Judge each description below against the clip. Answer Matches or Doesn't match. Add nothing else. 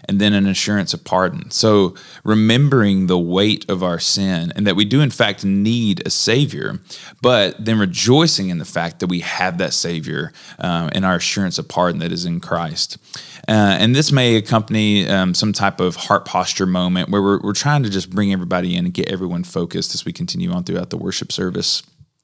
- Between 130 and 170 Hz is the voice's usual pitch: Doesn't match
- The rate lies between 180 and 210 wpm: Matches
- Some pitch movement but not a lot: Matches